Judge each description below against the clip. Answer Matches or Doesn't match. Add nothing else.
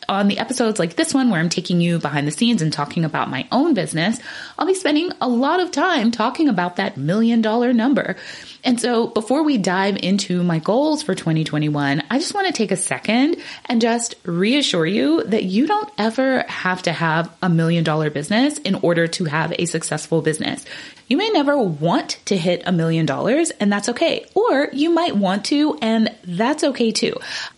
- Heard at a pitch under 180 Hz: Doesn't match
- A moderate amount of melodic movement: Doesn't match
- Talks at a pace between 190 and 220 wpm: Matches